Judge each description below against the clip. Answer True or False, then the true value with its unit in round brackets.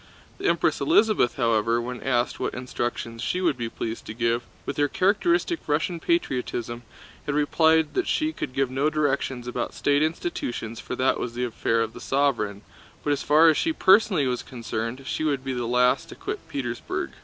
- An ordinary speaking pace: True (185 wpm)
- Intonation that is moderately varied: True (4.6 semitones)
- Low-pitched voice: True (130 Hz)